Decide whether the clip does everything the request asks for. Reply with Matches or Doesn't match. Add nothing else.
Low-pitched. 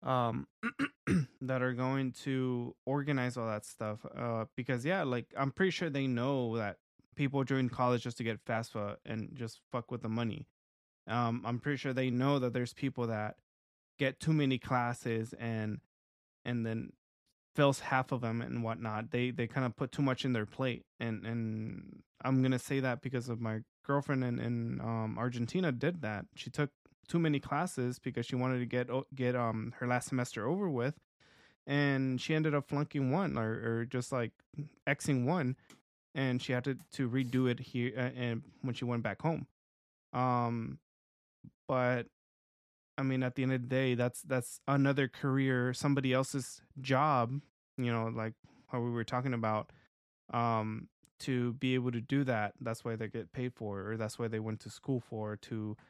Matches